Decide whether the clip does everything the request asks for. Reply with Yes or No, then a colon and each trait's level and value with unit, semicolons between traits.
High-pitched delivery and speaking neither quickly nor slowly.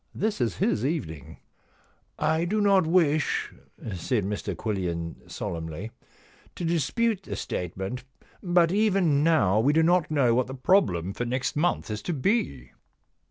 No: low, 135 Hz; average, 155 wpm